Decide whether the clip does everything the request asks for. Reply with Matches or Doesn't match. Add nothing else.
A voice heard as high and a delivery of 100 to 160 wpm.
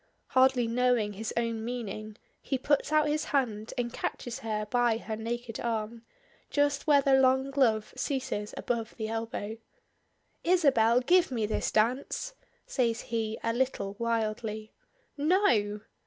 Matches